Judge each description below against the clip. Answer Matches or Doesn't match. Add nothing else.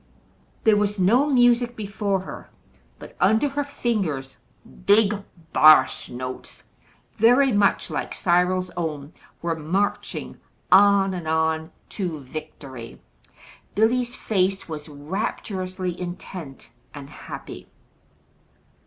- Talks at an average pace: Doesn't match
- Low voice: Doesn't match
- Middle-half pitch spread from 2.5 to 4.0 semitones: Doesn't match